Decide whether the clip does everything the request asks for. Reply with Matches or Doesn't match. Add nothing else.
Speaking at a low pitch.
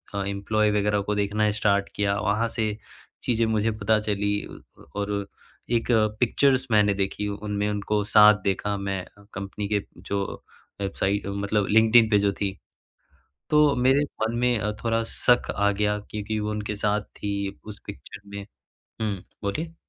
Matches